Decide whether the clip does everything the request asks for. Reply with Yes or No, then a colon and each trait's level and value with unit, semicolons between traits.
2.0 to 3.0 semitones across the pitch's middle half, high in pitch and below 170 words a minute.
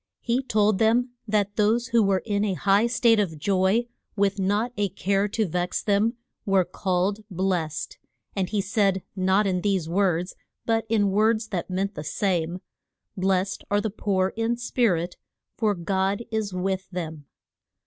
Yes: average, 2.7 semitones; high, 200 Hz; average, 160 wpm